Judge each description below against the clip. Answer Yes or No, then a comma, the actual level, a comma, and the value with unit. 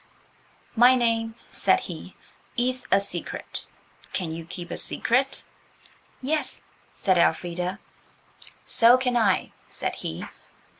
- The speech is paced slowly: Yes, slow, 110 wpm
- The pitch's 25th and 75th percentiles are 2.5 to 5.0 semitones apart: No, wide, 5.6 semitones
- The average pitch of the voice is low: No, high, 230 Hz